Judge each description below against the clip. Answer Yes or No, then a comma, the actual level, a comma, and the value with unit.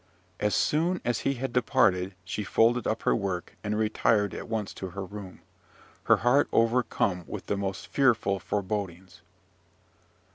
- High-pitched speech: No, low, 105 Hz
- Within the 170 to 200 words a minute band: No, average, 150 wpm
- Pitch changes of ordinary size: Yes, average, 3.7 semitones